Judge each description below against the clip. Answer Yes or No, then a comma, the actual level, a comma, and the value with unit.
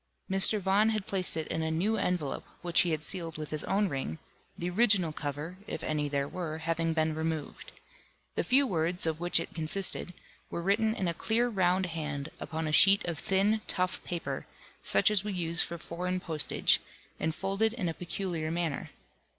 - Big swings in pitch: No, average, 3.4 semitones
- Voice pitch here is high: No, medium, 175 Hz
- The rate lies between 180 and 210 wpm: Yes, average, 190 wpm